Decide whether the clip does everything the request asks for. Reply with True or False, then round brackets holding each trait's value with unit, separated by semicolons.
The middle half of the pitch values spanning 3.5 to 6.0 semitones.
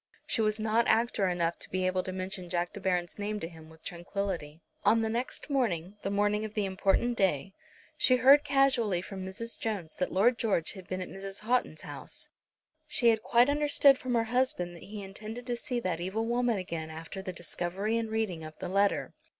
True (4.1 semitones)